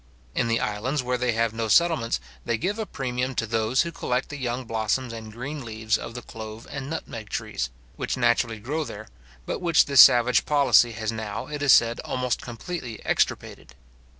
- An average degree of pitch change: Yes, average, 3.4 semitones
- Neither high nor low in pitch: No, low, 120 Hz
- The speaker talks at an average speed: Yes, average, 190 wpm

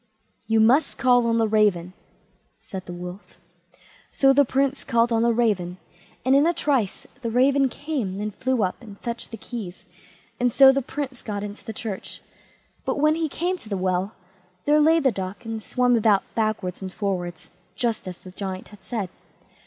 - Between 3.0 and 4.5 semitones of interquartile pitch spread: No, average, 5.2 semitones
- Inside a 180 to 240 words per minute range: Yes, average, 185 wpm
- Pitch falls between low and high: No, high, 225 Hz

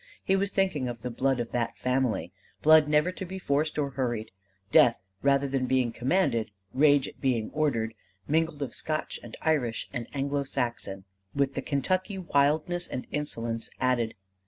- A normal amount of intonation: Yes, average, 4.2 semitones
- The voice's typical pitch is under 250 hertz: Yes, medium, 140 Hz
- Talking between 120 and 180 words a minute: Yes, average, 165 wpm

